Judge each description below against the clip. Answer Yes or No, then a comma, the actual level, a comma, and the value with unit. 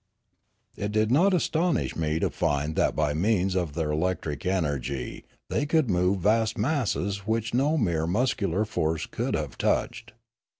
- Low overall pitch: Yes, very low, 95 Hz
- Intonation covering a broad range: Yes, wide, 6.2 semitones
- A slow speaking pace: No, average, 155 wpm